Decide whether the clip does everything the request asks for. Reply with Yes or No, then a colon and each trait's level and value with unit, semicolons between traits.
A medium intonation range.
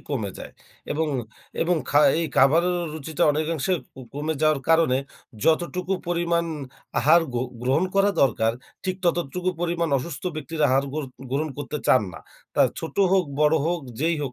Yes: average, 3.5 semitones